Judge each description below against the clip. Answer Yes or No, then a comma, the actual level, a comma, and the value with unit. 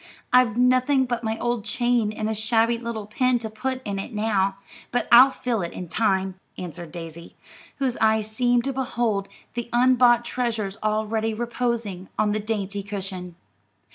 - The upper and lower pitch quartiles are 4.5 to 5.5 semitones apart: No, average, 3.0 semitones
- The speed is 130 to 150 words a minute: No, average, 165 wpm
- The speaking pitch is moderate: No, high, 220 Hz